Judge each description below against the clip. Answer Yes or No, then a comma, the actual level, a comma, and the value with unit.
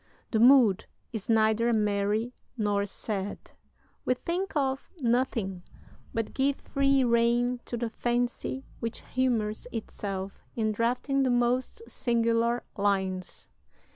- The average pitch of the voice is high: Yes, high, 235 Hz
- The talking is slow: Yes, slow, 115 wpm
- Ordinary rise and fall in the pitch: Yes, average, 3.0 semitones